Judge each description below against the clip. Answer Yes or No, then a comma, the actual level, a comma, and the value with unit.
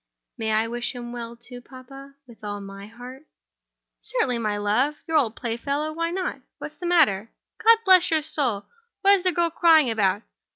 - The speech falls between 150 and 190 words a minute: Yes, average, 165 wpm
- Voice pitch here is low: No, very high, 255 Hz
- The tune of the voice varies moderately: No, wide, 6.0 semitones